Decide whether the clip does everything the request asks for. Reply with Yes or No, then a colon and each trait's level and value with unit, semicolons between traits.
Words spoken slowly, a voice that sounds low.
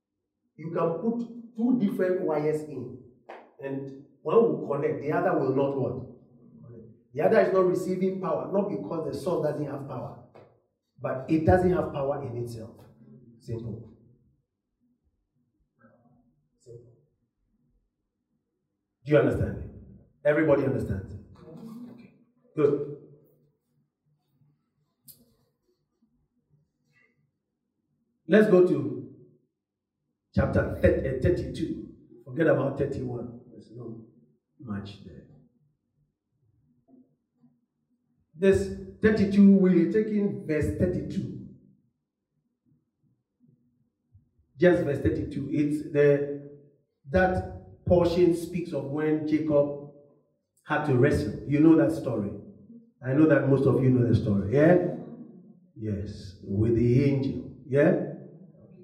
No: slow, 100 wpm; medium, 145 Hz